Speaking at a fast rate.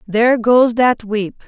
No: average, 160 wpm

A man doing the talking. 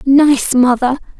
No: female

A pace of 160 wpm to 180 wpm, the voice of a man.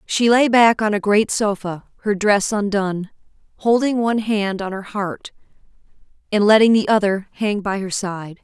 No: average, 170 wpm; female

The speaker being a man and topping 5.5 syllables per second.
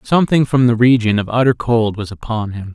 Yes: male; 5.7 syllables/s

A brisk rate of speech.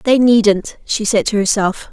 No: average, 190 wpm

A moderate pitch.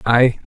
No: low, 115 Hz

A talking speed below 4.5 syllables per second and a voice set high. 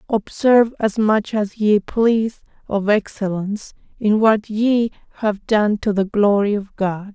Yes: 4.1 syllables/s; high, 210 Hz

